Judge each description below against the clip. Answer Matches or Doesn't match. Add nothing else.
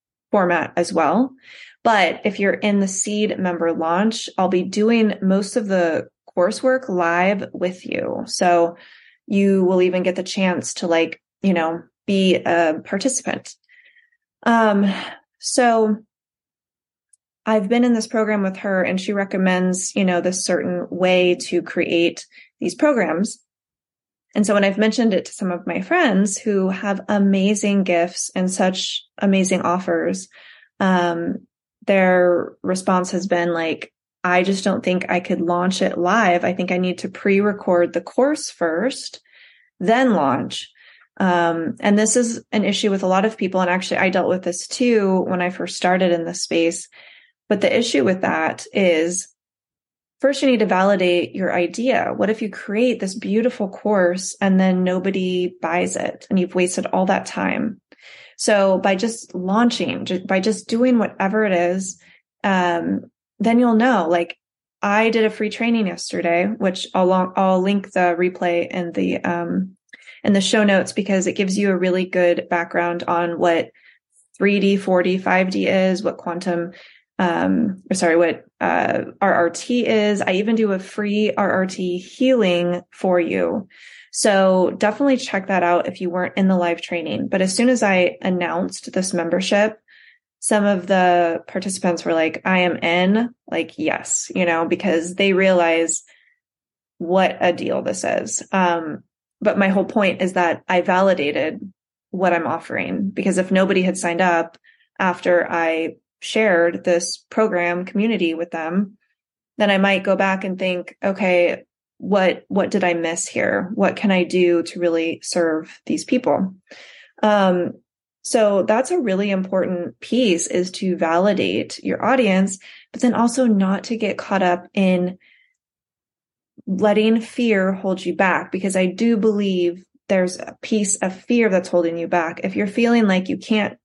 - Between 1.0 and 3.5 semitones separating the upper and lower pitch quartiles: Matches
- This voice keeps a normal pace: Matches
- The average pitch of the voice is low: Doesn't match